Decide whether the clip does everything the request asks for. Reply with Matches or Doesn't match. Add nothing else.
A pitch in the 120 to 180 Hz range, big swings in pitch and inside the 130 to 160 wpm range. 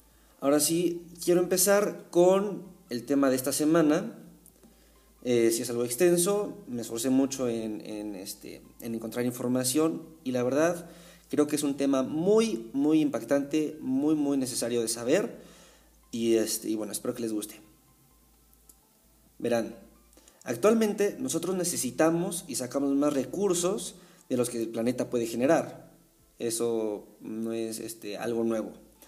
Matches